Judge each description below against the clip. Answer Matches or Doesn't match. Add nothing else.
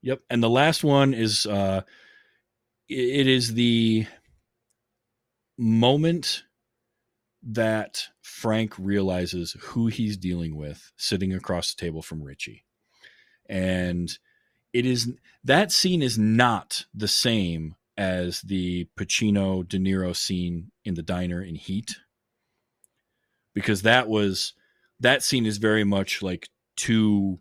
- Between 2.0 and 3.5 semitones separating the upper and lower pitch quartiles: Doesn't match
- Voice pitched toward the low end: Matches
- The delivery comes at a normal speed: Doesn't match